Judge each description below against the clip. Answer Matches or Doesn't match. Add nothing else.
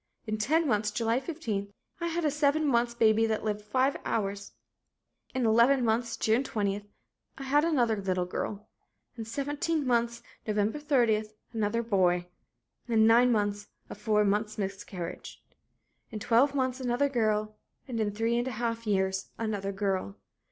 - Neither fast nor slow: Matches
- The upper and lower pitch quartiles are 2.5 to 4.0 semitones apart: Matches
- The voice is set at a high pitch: Matches